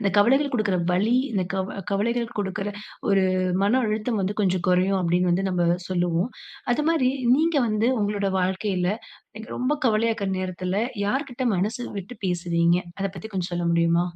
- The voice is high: Yes, high, 195 Hz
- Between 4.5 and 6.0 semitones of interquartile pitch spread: No, average, 3.7 semitones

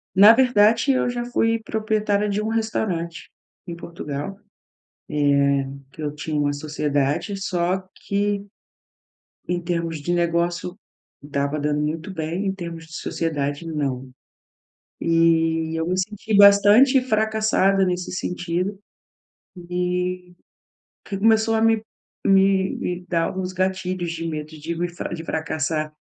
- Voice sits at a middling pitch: Yes, medium, 180 Hz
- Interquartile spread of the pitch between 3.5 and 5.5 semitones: Yes, average, 3.8 semitones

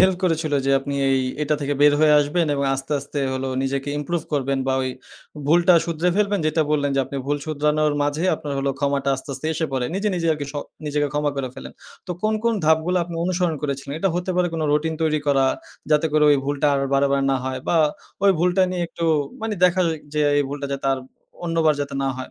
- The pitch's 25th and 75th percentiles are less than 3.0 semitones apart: No, average, 3.3 semitones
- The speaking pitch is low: No, medium, 150 Hz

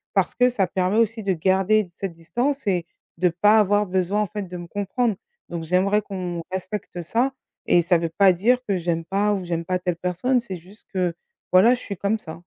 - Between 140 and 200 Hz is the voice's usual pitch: Yes, high, 190 Hz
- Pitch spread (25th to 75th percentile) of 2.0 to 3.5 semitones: Yes, average, 3.0 semitones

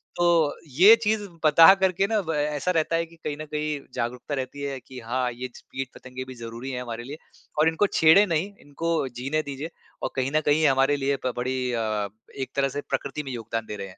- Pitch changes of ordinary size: Yes, average, 4.0 semitones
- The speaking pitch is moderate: Yes, medium, 145 Hz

